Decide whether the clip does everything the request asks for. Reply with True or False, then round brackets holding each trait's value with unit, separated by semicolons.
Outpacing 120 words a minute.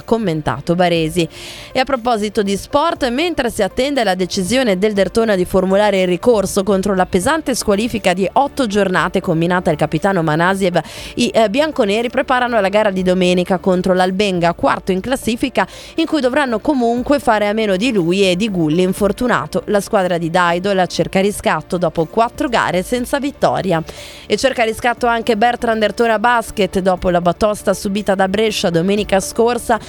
True (160 wpm)